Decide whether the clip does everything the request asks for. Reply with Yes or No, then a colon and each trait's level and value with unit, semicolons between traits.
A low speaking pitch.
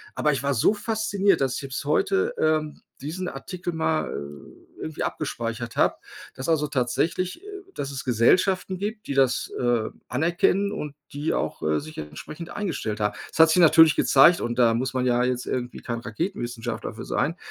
No: medium, 145 Hz